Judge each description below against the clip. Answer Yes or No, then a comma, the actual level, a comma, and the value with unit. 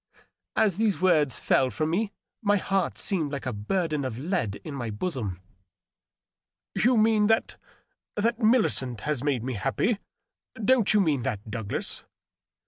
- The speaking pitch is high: No, medium, 155 Hz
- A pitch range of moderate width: No, wide, 8.6 semitones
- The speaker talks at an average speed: Yes, average, 155 wpm